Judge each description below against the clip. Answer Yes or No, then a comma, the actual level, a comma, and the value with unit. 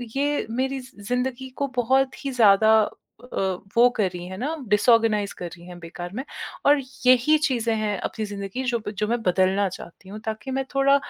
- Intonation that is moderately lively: Yes, average, 4.7 semitones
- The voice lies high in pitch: Yes, high, 230 Hz